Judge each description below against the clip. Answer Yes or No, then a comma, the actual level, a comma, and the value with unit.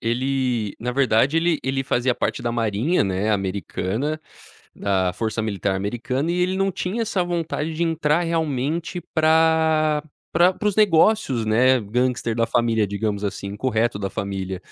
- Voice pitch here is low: Yes, low, 130 Hz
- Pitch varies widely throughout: Yes, wide, 6.9 semitones